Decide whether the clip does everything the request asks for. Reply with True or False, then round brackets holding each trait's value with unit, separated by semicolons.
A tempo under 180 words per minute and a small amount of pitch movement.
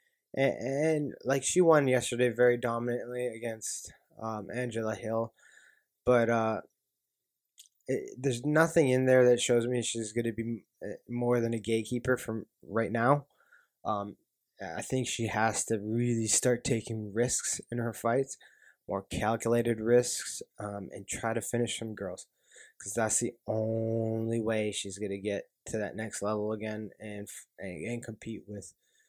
True (155 wpm; 1.9 semitones)